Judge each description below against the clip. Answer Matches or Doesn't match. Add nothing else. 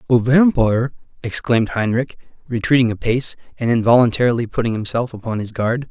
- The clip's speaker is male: Matches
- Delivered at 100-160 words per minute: Matches